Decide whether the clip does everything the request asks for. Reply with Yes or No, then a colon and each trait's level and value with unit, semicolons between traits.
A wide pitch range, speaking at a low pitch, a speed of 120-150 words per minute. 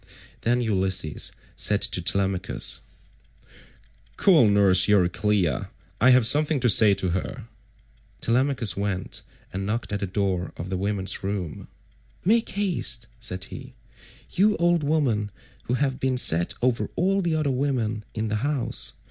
Yes: wide, 5.8 semitones; low, 110 Hz; average, 140 wpm